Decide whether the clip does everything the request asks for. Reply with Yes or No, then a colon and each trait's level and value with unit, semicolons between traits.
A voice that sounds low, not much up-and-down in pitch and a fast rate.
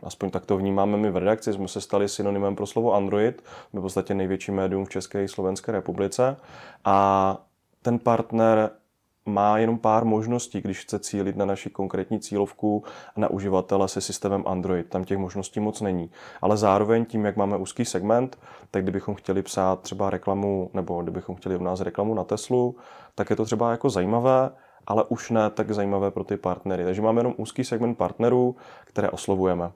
Yes: low, 100 Hz; narrow, 2.3 semitones; fast, 185 wpm